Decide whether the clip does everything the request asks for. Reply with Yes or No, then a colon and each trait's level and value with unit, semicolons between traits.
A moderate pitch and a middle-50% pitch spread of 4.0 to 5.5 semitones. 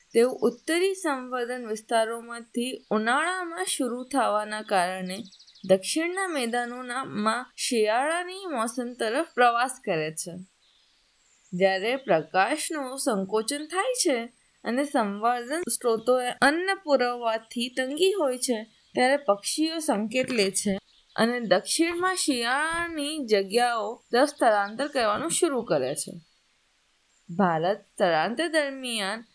No: high, 245 Hz; average, 5.2 semitones